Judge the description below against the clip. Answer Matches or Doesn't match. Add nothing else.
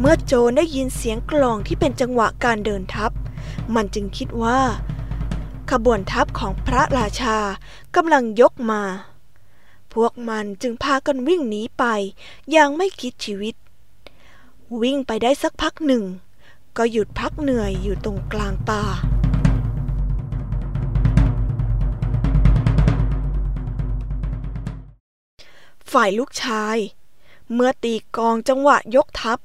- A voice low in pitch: Doesn't match